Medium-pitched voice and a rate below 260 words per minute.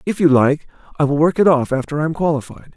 No: medium, 155 Hz; fast, 285 wpm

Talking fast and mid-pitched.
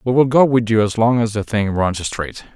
No: fast, 280 wpm; low, 115 Hz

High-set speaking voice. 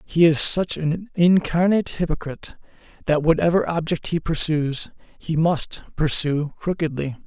No: medium, 160 Hz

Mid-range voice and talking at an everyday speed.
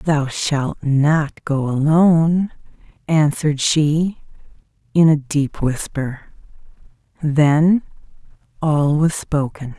No: medium, 150 Hz; slow, 90 wpm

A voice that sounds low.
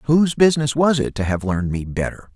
Yes: low, 130 Hz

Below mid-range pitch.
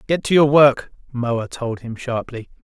Yes: low, 130 Hz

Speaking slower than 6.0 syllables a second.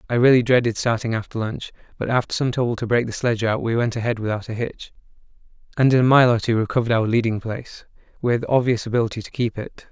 No: 6.7 syllables/s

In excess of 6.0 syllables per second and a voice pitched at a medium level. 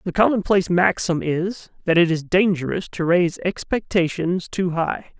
No: 4.7 syllables/s; medium, 180 Hz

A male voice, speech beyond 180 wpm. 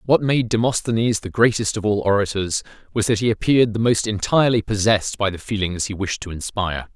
Yes: male; average, 200 wpm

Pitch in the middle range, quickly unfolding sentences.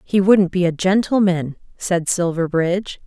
No: medium, 180 Hz; slow, 135 wpm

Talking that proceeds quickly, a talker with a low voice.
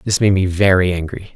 Yes: fast, 220 wpm; very low, 95 Hz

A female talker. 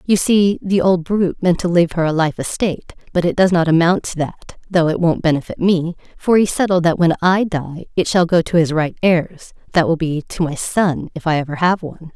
Yes: female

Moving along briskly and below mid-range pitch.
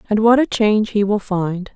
No: fast, 240 wpm; high, 210 Hz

